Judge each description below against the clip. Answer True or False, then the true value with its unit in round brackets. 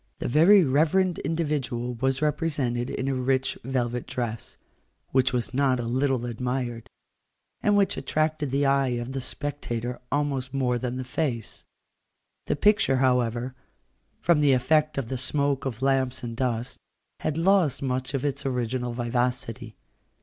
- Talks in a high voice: False (130 Hz)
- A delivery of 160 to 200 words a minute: False (150 wpm)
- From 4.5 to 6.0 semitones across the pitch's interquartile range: False (2.9 semitones)